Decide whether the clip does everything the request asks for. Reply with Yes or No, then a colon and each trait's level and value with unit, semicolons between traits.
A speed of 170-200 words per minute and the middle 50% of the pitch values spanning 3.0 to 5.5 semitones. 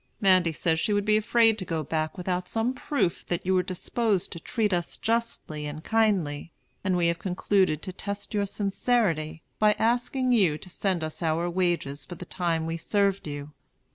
Yes: average, 190 wpm; average, 4.3 semitones